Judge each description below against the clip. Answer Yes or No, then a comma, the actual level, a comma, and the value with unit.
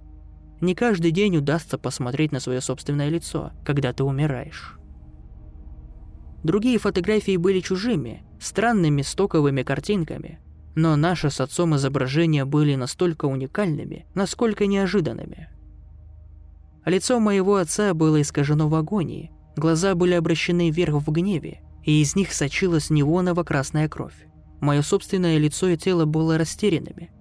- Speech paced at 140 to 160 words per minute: No, average, 120 wpm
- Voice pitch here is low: No, medium, 155 Hz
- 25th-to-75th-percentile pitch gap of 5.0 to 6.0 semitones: Yes, wide, 5.6 semitones